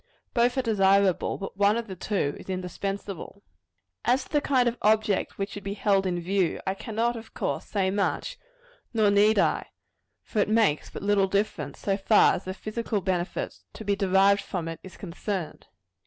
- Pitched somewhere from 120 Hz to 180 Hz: No, high, 200 Hz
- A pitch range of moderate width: No, narrow, 2.2 semitones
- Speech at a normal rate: Yes, average, 185 wpm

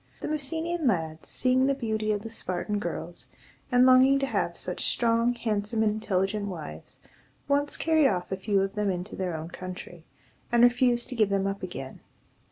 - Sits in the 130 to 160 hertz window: No, high, 215 Hz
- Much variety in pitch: No, average, 4.9 semitones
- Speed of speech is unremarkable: Yes, average, 180 wpm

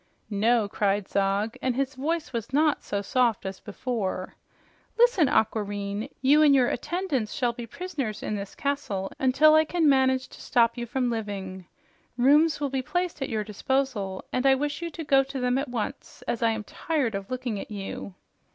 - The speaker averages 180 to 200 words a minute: Yes, average, 190 wpm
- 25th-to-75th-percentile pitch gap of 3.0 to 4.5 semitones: No, average, 5.1 semitones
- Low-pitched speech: No, very high, 250 Hz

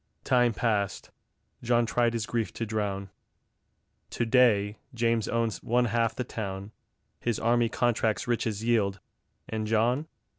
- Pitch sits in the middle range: No, low, 115 Hz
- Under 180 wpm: Yes, slow, 135 wpm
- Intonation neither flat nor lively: No, narrow, 1.9 semitones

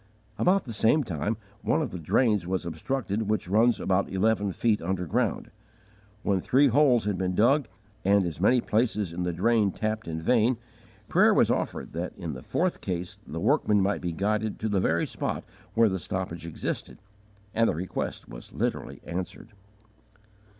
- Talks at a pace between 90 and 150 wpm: No, average, 170 wpm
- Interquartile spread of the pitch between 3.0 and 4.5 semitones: Yes, average, 4.2 semitones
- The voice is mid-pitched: No, low, 100 Hz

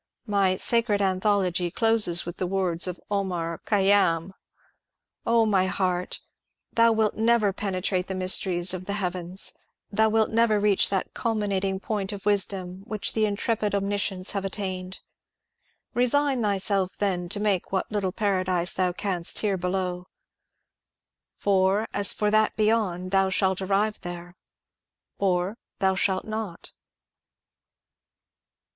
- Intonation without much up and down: Yes, narrow, 2.3 semitones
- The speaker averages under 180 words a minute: Yes, average, 140 wpm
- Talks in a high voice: Yes, high, 195 Hz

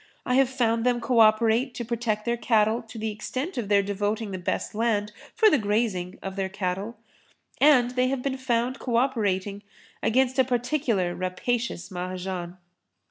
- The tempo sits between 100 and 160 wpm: No, average, 170 wpm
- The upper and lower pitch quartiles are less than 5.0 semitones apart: Yes, average, 3.6 semitones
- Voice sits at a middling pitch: No, high, 225 Hz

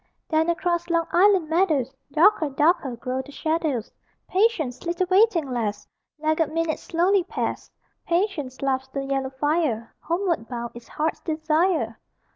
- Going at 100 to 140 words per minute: Yes, slow, 135 wpm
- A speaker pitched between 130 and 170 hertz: No, very high, 315 Hz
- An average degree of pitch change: Yes, average, 4.6 semitones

